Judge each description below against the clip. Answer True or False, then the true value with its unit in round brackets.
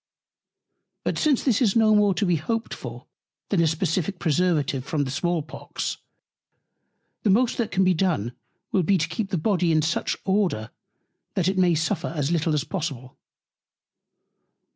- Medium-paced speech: True (165 wpm)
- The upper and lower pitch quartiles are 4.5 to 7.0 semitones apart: False (4.1 semitones)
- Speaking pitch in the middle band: True (175 Hz)